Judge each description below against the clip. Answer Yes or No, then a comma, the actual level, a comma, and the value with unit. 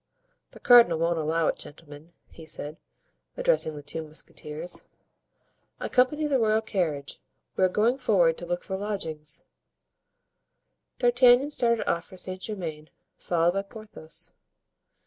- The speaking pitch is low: No, medium, 180 Hz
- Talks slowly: Yes, slow, 130 wpm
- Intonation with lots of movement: Yes, wide, 5.8 semitones